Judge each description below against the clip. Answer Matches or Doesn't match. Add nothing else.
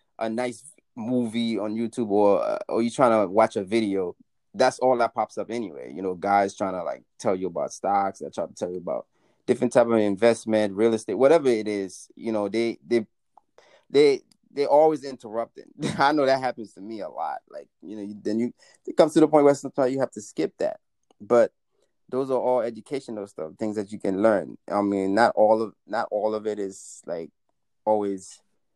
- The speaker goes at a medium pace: Doesn't match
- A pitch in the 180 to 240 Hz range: Doesn't match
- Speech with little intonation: Doesn't match